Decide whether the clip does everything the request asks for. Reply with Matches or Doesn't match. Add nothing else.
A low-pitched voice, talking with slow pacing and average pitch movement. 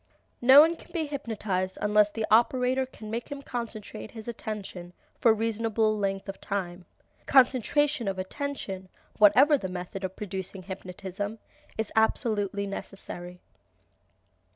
Doesn't match